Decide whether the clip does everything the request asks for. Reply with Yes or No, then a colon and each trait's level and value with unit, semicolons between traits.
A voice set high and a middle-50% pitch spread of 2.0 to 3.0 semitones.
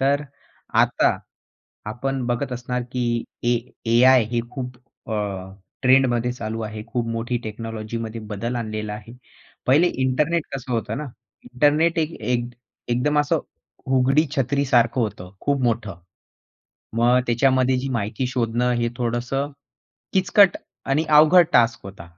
No: low, 125 Hz; average, 2.7 semitones